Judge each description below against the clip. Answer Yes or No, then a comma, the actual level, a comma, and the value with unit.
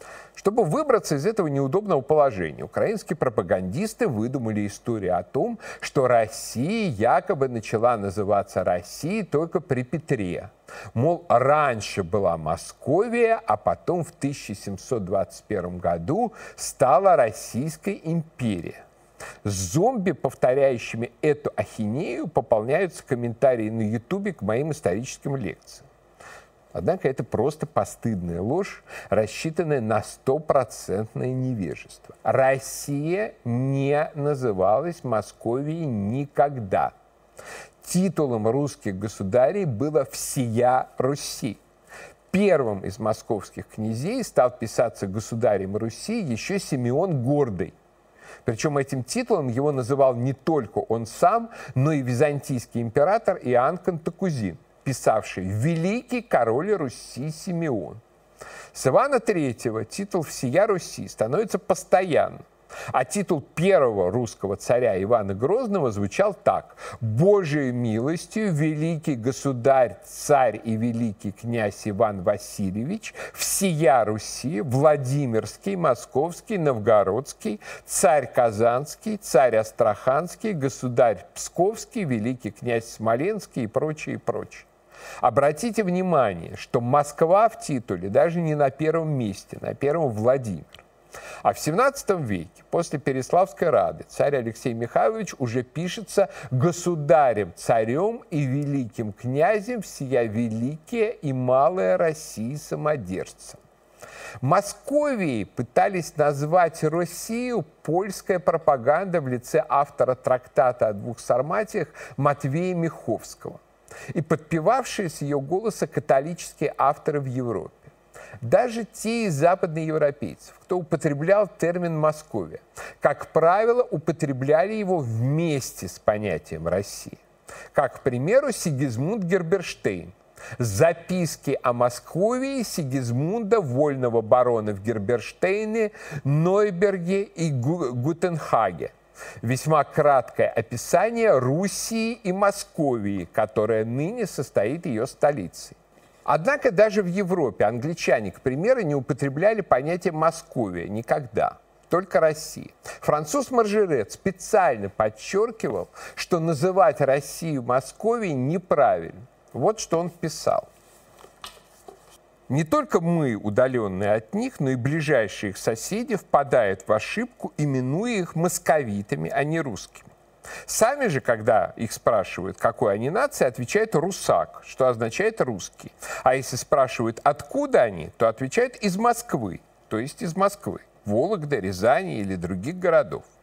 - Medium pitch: Yes, medium, 145 Hz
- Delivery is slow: Yes, slow, 105 wpm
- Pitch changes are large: Yes, wide, 7.2 semitones